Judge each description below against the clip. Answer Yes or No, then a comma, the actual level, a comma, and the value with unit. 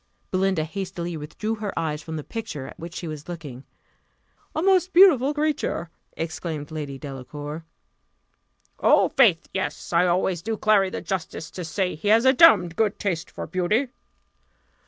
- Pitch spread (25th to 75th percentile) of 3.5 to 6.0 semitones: Yes, wide, 5.4 semitones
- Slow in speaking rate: No, average, 155 wpm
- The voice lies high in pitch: No, medium, 175 Hz